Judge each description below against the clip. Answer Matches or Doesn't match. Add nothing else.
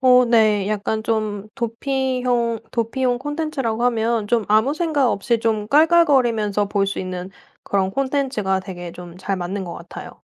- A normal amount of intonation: Matches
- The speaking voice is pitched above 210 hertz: Matches